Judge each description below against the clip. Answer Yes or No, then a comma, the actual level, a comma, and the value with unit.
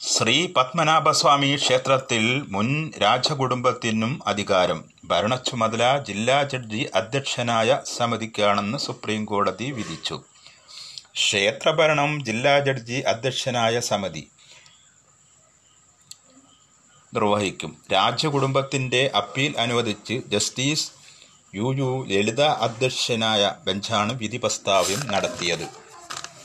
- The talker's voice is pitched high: No, low, 125 Hz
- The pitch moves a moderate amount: Yes, average, 4.0 semitones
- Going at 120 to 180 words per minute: No, average, 75 wpm